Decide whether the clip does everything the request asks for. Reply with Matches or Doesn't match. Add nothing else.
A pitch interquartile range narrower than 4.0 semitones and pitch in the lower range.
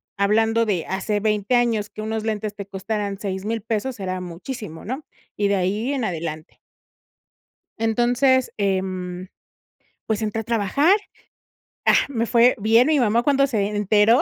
Doesn't match